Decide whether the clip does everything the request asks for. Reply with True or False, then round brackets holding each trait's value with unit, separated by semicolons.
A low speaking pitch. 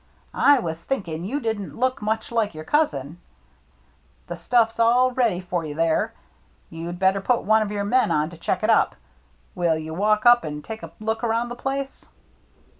False (215 Hz)